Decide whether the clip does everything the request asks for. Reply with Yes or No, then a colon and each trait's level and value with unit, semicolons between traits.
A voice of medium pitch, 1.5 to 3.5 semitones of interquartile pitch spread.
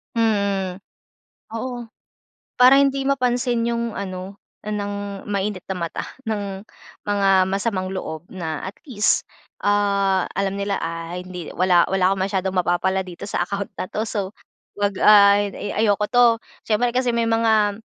No: high, 200 Hz; average, 2.8 semitones